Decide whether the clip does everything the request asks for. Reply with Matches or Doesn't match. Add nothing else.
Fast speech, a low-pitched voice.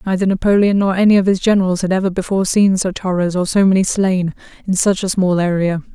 Doesn't match